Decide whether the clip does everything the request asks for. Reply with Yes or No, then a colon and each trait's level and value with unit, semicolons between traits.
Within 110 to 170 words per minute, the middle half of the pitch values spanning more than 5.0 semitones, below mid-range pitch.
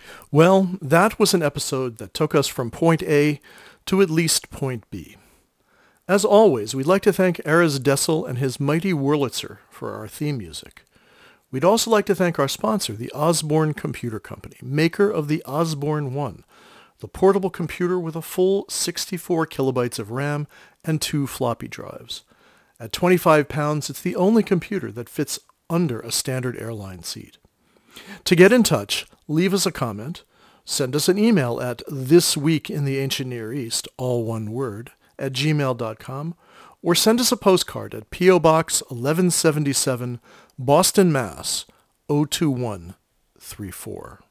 No: average, 150 wpm; wide, 5.4 semitones; medium, 150 Hz